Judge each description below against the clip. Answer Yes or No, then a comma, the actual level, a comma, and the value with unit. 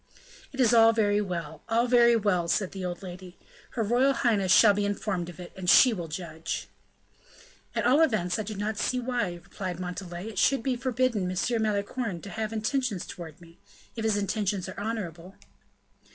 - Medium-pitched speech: No, high, 205 Hz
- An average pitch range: Yes, average, 4.2 semitones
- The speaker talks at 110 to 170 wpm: No, average, 185 wpm